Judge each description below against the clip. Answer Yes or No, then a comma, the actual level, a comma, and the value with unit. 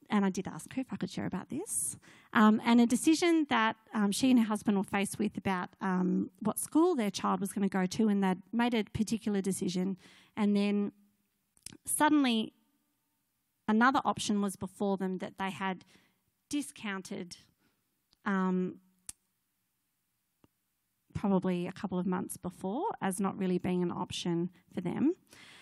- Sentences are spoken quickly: No, average, 160 wpm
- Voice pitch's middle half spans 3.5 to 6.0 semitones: No, average, 3.1 semitones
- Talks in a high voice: Yes, high, 200 Hz